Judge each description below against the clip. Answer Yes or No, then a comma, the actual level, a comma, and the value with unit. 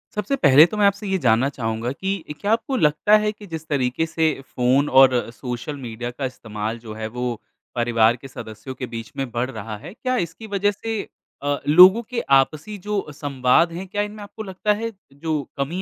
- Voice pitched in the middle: Yes, medium, 145 Hz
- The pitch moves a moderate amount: No, wide, 8.4 semitones